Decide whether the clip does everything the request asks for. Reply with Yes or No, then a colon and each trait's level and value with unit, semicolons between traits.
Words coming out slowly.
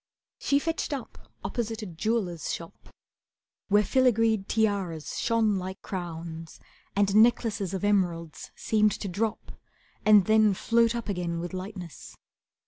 Yes: slow, 130 wpm